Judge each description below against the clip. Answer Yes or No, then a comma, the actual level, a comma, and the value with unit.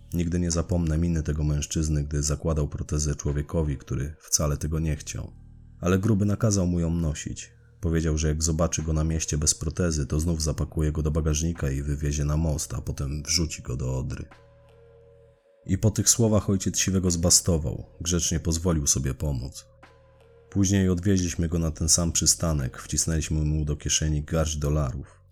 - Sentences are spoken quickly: Yes, fast, 165 wpm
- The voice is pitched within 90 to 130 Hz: No, very low, 80 Hz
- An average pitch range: Yes, average, 3.2 semitones